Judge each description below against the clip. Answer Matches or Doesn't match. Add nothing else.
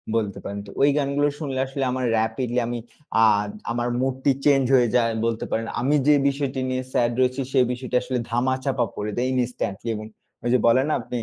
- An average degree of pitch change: Doesn't match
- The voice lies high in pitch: Doesn't match